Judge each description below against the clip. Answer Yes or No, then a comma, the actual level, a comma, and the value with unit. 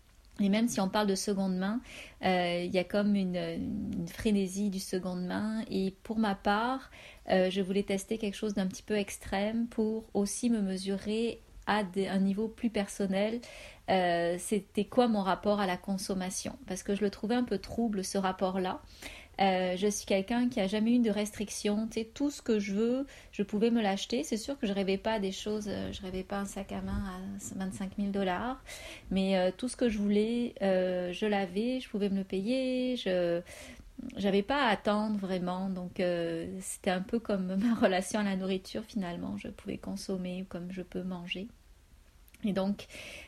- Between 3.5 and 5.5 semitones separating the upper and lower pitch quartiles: No, average, 2.7 semitones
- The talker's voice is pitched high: Yes, high, 200 Hz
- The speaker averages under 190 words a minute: No, average, 200 wpm